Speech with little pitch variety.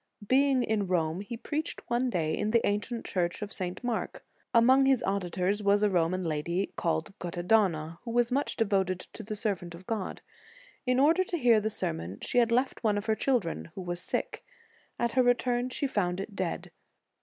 No: average, 5.2 semitones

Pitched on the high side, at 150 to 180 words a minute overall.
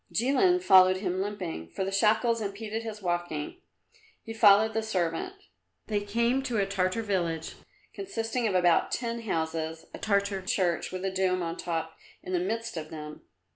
Yes: high, 195 Hz; average, 170 wpm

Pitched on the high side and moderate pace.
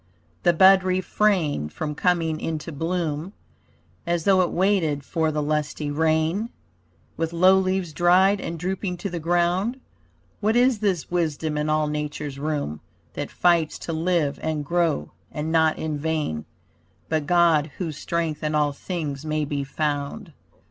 No: medium, 160 Hz; average, 150 wpm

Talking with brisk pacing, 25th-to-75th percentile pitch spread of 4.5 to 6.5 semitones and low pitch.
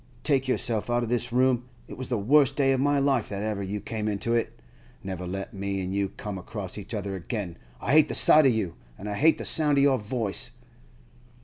Yes: fast, 230 wpm; average, 4.9 semitones; low, 110 Hz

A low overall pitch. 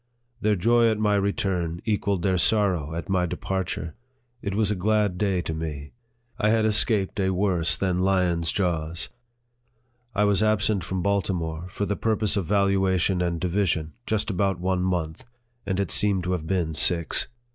Yes: very low, 95 Hz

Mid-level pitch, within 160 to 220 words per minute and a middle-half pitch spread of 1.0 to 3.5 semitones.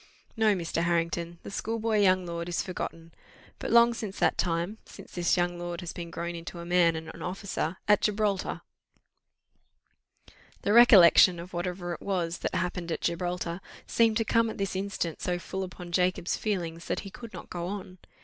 Yes: medium, 180 Hz; average, 190 wpm; average, 2.7 semitones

